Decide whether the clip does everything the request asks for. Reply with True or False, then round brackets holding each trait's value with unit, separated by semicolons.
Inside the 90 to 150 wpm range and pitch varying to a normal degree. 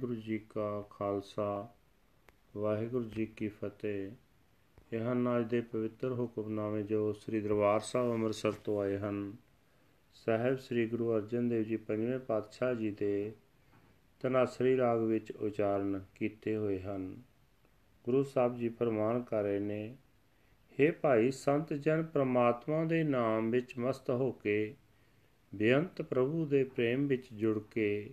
True (135 wpm; 3.1 semitones)